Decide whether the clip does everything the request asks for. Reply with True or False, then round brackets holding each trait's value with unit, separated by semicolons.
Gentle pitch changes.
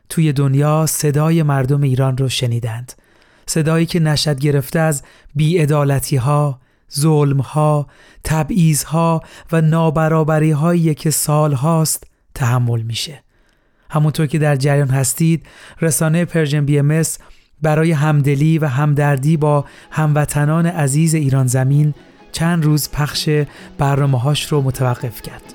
True (2.1 semitones)